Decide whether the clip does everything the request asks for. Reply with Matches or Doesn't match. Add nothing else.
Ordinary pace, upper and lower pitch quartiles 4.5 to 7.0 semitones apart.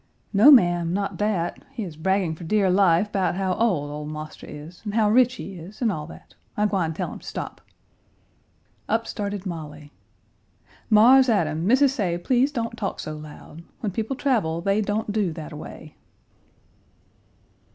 Matches